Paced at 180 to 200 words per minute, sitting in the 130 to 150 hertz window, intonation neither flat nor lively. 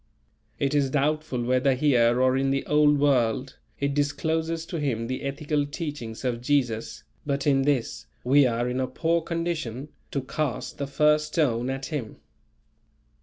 No: average, 160 wpm; medium, 140 Hz; average, 3.0 semitones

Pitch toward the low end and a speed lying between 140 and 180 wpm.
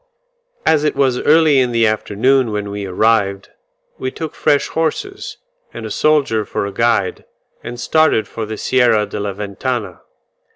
Yes: low, 115 Hz; average, 160 wpm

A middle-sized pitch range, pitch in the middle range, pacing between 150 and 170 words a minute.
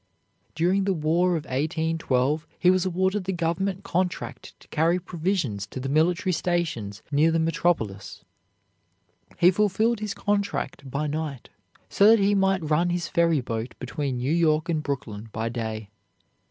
Yes: average, 4.8 semitones; medium, 165 Hz; average, 155 wpm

